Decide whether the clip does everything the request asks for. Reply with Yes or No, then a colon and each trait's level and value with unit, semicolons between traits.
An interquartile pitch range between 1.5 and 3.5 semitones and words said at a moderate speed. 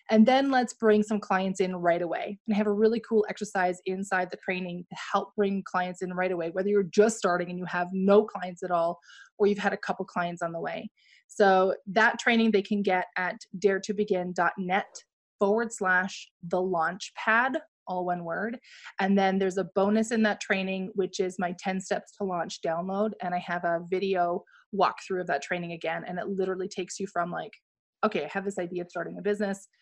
No: narrow, 2.5 semitones; fast, 210 wpm